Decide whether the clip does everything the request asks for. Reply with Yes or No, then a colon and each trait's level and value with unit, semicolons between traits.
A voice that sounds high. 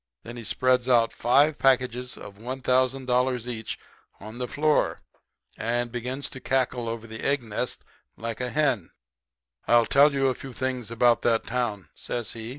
No: low, 125 Hz